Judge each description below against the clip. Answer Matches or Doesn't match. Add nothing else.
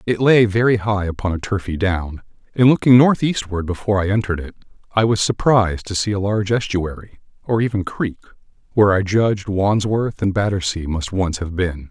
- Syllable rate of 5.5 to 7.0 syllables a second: Matches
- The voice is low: Matches